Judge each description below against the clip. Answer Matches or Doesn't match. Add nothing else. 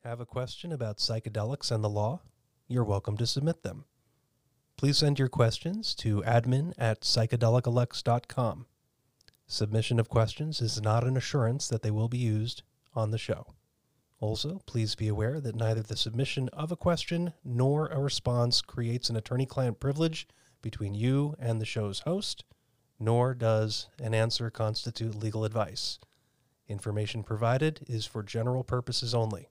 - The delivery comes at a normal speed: Matches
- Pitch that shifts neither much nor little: Matches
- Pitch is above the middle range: Doesn't match